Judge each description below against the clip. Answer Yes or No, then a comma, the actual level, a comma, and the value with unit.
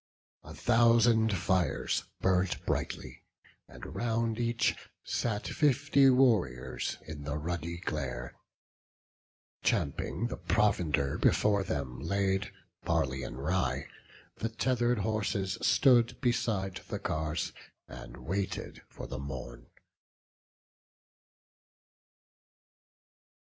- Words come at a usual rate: No, slow, 90 wpm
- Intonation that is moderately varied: No, wide, 7.5 semitones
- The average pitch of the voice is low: Yes, very low, 95 Hz